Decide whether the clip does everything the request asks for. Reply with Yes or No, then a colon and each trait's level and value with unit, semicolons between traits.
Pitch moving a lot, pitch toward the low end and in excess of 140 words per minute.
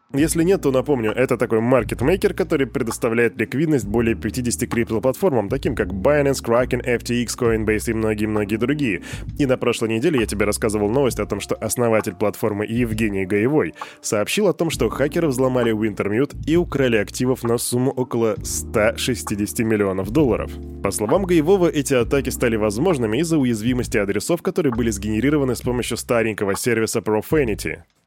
No: average, 3.6 semitones; low, 120 Hz; average, 150 wpm